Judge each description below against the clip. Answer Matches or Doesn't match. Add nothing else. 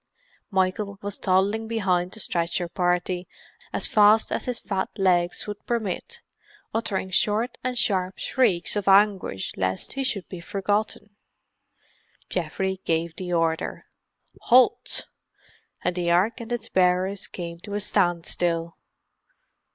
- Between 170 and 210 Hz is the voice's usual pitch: Matches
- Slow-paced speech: Matches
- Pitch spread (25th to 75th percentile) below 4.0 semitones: Matches